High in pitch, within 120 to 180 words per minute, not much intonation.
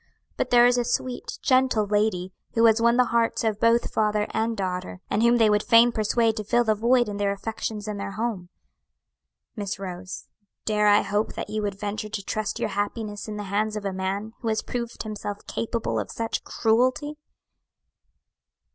No: high, 215 Hz; average, 190 wpm; narrow, 2.2 semitones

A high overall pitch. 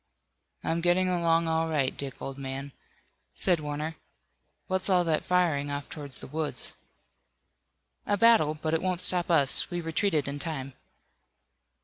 No: medium, 160 Hz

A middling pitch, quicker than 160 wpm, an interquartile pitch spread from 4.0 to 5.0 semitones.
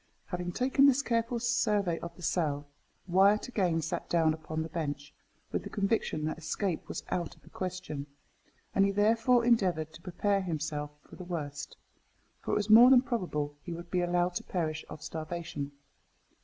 Yes: medium, 175 Hz; average, 180 wpm; average, 4.7 semitones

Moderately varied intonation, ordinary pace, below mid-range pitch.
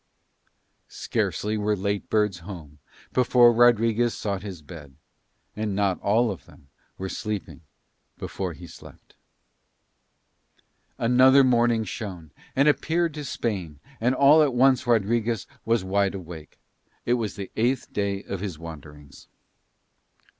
No: average, 4.4 semitones; slow, 125 wpm; low, 105 Hz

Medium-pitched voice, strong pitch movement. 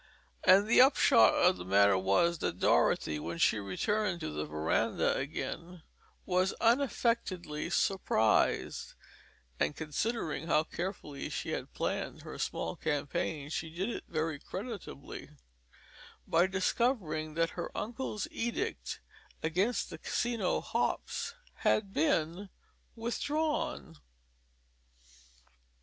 Yes: medium, 175 Hz; wide, 6.6 semitones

